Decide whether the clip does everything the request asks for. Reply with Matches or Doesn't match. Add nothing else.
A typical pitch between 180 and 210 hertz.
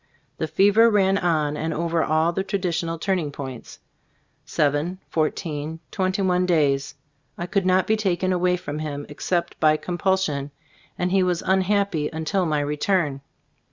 Doesn't match